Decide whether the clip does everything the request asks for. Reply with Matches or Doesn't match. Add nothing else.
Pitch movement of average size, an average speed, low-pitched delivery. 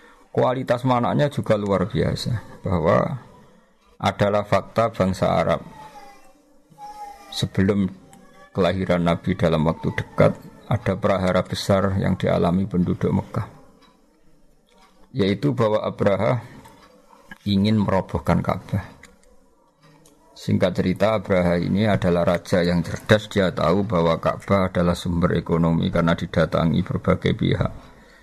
Matches